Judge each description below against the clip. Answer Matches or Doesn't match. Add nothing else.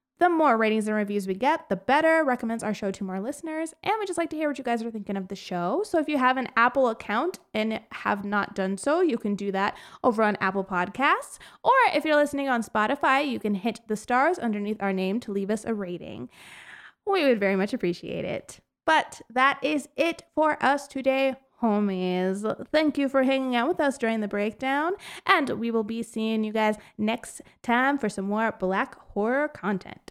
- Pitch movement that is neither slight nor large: Doesn't match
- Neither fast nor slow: Doesn't match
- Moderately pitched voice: Doesn't match